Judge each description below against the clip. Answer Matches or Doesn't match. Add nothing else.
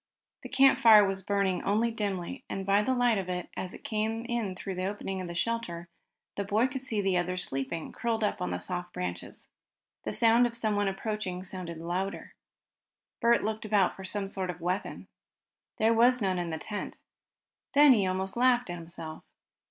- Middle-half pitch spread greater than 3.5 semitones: Matches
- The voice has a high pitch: Matches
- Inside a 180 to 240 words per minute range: Matches